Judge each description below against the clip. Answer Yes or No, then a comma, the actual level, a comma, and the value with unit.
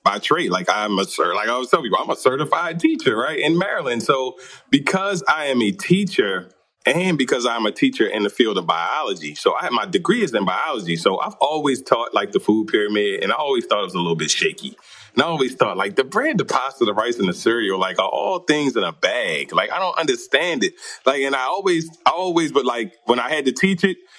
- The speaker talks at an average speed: No, fast, 245 wpm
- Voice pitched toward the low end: No, high, 190 Hz